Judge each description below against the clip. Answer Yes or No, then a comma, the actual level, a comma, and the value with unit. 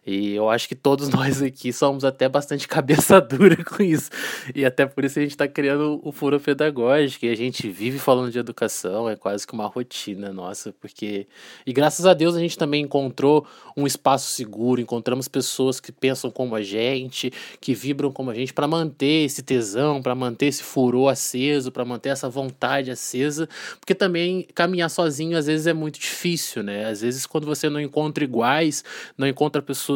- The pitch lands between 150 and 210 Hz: No, medium, 140 Hz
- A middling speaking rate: No, fast, 190 wpm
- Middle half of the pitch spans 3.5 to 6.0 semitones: No, average, 3.1 semitones